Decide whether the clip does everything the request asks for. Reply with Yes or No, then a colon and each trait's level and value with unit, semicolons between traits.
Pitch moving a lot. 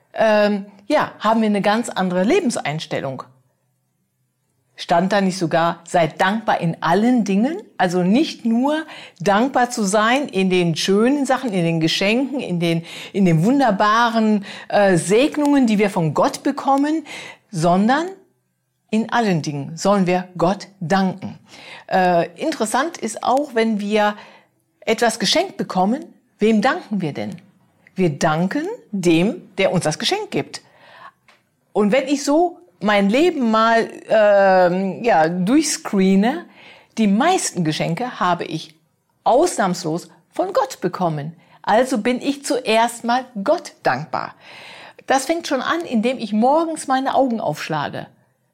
Yes: wide, 6.1 semitones